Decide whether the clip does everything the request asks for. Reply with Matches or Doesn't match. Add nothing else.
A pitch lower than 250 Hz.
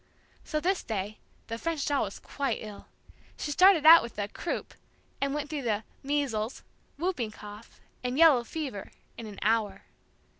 Doesn't match